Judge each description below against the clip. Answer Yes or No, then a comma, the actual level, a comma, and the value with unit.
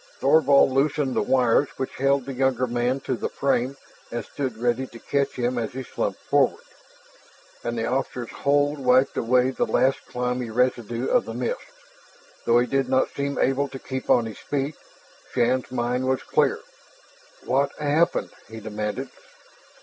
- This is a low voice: Yes, low, 130 Hz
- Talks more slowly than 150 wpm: No, average, 165 wpm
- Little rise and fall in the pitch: Yes, narrow, 2.2 semitones